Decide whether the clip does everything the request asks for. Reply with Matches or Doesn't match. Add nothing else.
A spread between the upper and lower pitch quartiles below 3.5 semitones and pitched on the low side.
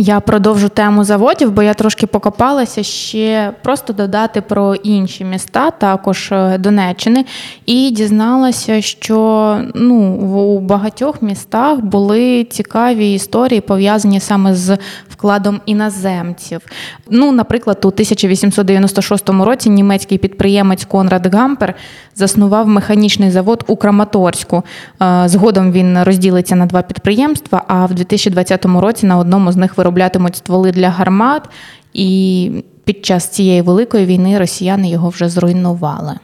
Doesn't match